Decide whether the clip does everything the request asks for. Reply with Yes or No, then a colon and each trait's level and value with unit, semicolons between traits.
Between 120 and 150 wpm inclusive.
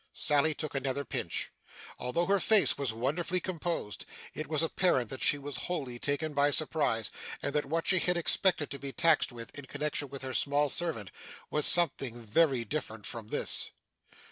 No: average, 175 wpm